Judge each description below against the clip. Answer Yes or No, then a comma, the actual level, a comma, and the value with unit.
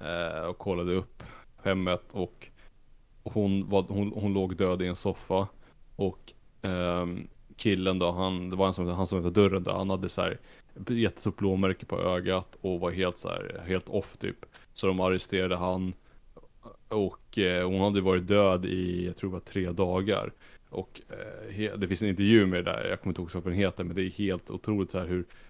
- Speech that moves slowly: No, fast, 195 wpm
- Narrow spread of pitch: Yes, narrow, 1.7 semitones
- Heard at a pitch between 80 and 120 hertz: Yes, very low, 95 Hz